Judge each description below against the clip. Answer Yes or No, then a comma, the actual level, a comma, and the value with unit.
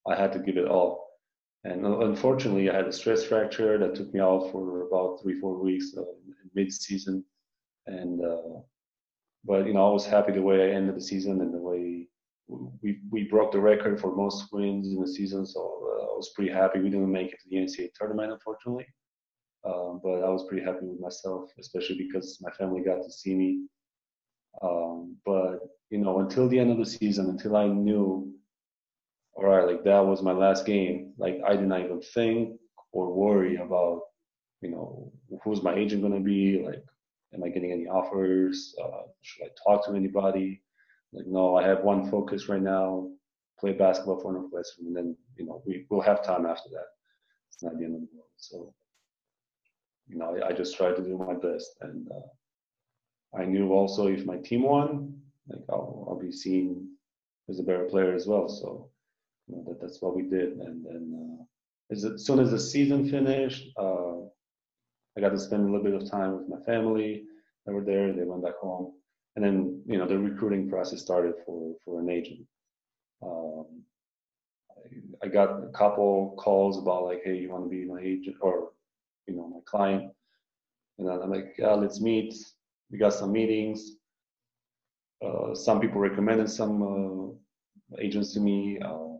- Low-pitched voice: Yes, very low, 95 Hz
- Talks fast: No, average, 190 wpm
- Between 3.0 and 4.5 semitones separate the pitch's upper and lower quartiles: No, narrow, 2.4 semitones